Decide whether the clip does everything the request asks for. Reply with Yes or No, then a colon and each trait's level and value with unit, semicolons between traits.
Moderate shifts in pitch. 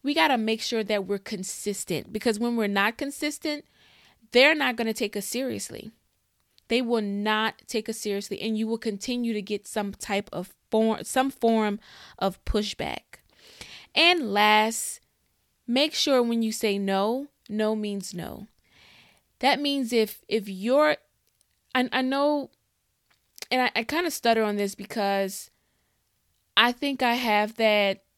Yes: average, 3.5 semitones